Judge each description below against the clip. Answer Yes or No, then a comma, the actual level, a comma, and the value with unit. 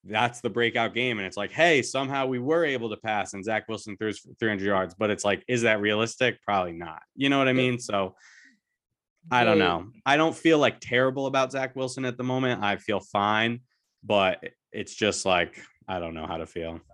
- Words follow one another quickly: Yes, fast, 215 wpm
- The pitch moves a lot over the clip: No, average, 4.1 semitones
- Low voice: Yes, low, 115 Hz